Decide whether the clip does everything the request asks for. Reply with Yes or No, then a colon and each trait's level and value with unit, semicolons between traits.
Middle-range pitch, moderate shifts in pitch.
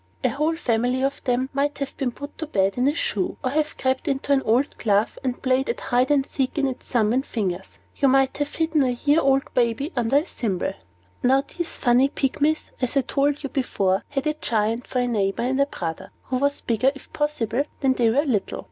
No: very high, 265 Hz; average, 3.2 semitones